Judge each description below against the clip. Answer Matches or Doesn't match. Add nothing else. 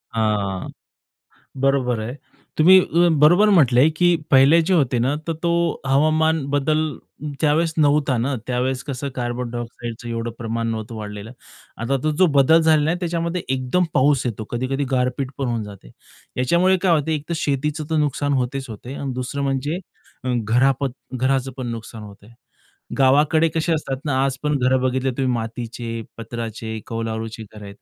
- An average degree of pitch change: Matches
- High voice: Doesn't match